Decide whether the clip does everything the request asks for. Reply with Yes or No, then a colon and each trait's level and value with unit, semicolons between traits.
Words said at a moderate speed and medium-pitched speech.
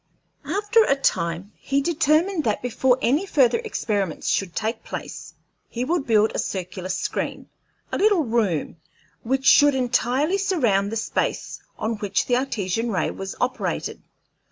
No: average, 145 wpm; high, 245 Hz